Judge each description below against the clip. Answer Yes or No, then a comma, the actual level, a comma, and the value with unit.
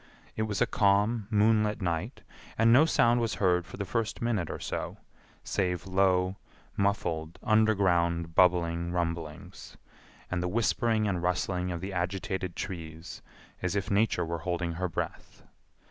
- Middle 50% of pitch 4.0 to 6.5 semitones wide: No, average, 3.6 semitones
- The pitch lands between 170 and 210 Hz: No, very low, 95 Hz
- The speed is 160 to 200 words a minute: No, average, 145 wpm